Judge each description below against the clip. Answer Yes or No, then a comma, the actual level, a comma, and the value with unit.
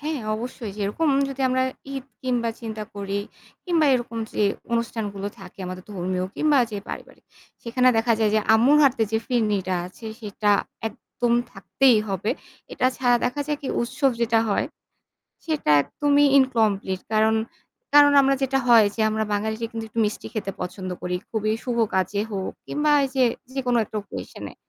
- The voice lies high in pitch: Yes, high, 230 Hz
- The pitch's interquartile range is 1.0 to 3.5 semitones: No, average, 4.2 semitones